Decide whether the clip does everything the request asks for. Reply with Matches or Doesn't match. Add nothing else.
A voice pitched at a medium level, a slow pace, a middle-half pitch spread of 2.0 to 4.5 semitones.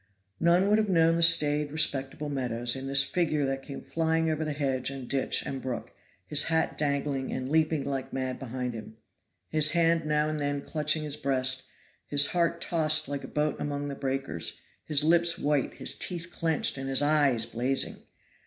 Doesn't match